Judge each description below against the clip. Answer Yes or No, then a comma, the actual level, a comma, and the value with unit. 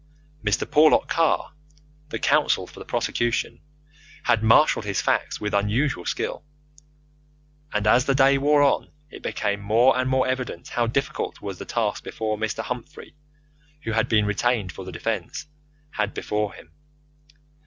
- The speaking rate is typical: Yes, average, 155 wpm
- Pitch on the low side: Yes, low, 115 Hz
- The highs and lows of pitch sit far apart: No, average, 4.0 semitones